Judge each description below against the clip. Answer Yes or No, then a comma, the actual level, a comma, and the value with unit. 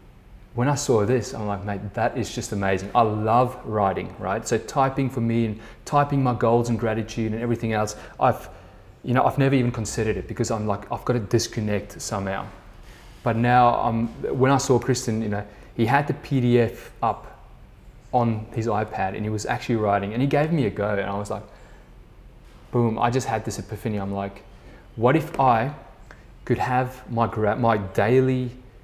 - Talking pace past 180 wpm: Yes, average, 190 wpm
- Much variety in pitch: No, average, 3.2 semitones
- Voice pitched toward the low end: Yes, low, 115 Hz